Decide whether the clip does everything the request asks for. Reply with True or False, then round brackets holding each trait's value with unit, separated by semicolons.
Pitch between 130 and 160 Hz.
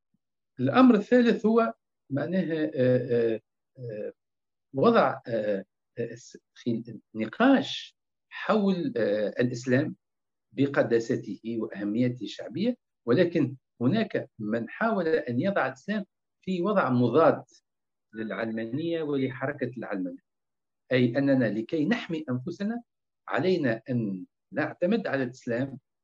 True (140 Hz)